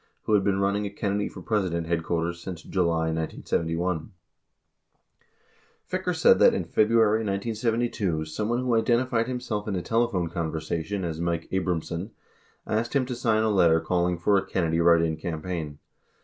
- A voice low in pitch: Yes, very low, 95 Hz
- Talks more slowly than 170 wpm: Yes, average, 160 wpm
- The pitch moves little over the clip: No, average, 4.6 semitones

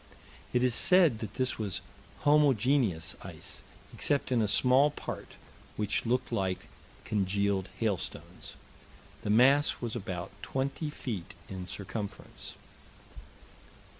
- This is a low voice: Yes, low, 115 Hz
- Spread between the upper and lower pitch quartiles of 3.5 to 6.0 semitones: Yes, average, 5.0 semitones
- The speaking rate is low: Yes, slow, 110 wpm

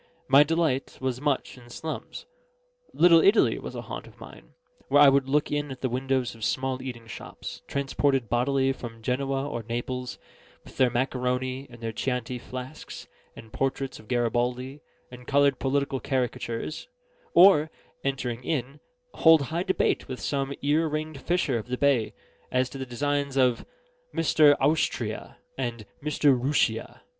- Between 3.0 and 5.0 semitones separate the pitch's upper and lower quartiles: No, narrow, 2.5 semitones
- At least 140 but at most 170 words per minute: Yes, average, 150 wpm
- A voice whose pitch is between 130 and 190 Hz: Yes, low, 135 Hz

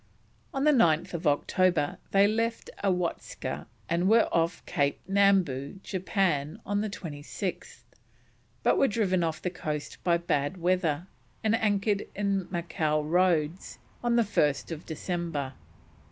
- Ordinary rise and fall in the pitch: Yes, average, 4.3 semitones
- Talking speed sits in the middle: No, slow, 120 wpm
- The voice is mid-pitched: Yes, medium, 180 Hz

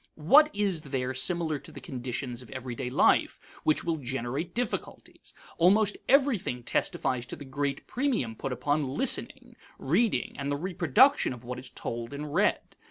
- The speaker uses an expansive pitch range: Yes, wide, 6.0 semitones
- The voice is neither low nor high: Yes, medium, 145 Hz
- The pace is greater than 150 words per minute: Yes, average, 160 wpm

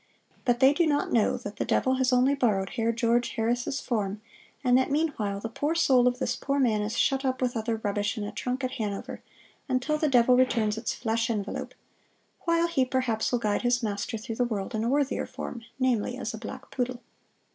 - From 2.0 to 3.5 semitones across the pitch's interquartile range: Yes, average, 2.9 semitones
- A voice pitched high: Yes, high, 245 Hz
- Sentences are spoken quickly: Yes, fast, 210 wpm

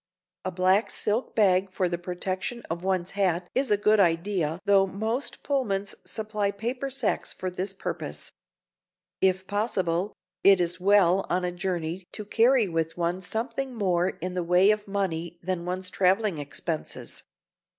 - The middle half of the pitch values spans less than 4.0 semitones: Yes, average, 2.7 semitones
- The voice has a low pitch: No, high, 190 Hz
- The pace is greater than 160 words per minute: No, average, 155 wpm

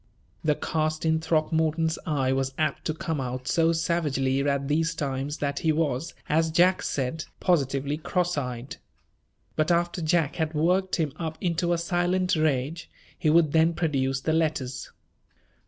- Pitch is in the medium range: Yes, medium, 155 Hz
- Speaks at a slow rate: No, average, 155 wpm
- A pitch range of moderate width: Yes, average, 3.1 semitones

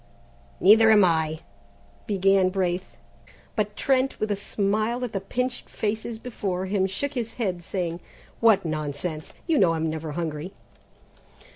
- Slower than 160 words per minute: Yes, average, 140 wpm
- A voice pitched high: Yes, high, 195 Hz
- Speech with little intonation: No, average, 4.2 semitones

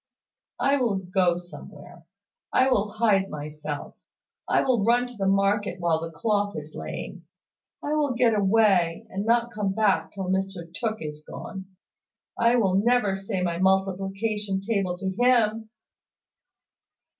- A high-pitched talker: Yes, high, 195 Hz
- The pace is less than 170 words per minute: Yes, average, 145 wpm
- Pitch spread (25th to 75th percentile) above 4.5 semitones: No, average, 3.4 semitones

